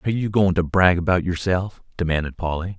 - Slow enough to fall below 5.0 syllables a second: No, 5.9 syllables/s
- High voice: No, very low, 90 Hz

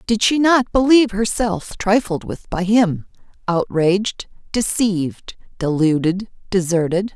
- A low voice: No, high, 200 Hz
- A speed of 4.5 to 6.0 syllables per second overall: No, 4.2 syllables/s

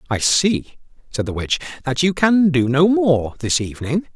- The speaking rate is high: No, average, 190 wpm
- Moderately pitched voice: Yes, medium, 145 Hz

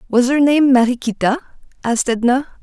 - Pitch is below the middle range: No, very high, 255 Hz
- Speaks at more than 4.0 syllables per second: Yes, 6.0 syllables/s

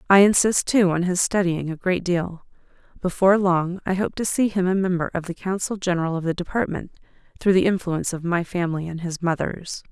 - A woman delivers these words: Yes, female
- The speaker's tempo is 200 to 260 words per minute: Yes, fast, 205 wpm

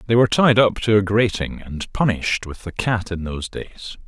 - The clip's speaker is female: No, male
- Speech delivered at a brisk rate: Yes, fast, 220 wpm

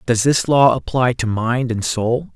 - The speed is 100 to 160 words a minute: No, fast, 205 wpm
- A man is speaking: Yes, male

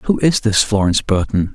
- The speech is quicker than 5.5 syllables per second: No, 5.3 syllables/s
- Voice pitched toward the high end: No, low, 110 Hz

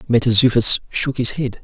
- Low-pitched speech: Yes, low, 120 Hz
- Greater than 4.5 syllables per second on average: Yes, 5.2 syllables/s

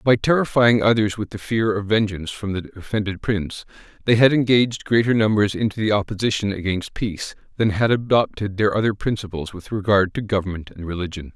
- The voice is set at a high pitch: No, low, 105 Hz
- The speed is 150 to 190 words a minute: Yes, average, 180 wpm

